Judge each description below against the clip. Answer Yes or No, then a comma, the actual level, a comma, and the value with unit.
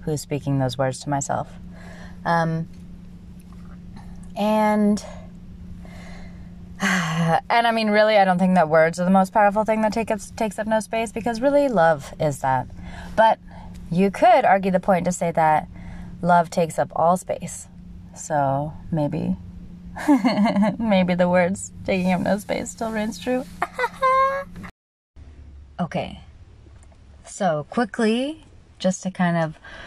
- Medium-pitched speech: Yes, medium, 170 Hz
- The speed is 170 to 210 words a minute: No, slow, 135 wpm